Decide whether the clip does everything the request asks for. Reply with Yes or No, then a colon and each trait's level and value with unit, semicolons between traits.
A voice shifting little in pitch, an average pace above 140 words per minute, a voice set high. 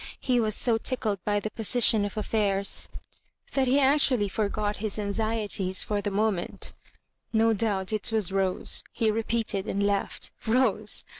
Yes: narrow, 1.9 semitones; average, 155 wpm; high, 215 Hz